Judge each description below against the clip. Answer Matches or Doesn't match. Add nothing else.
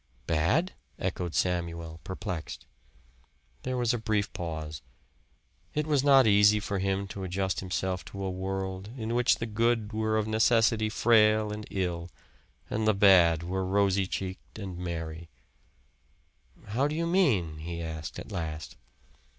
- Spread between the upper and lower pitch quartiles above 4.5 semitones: Doesn't match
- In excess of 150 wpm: Doesn't match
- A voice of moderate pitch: Doesn't match